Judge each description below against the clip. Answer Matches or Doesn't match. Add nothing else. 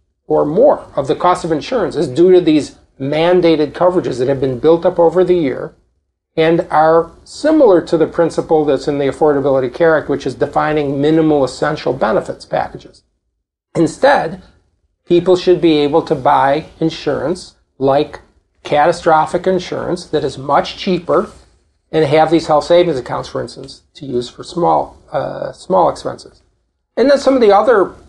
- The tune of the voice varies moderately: Matches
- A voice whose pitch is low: Doesn't match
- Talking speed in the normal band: Matches